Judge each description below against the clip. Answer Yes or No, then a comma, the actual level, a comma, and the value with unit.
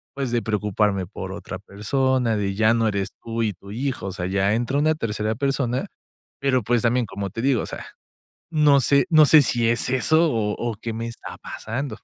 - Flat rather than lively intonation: No, average, 4.0 semitones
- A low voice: Yes, low, 115 Hz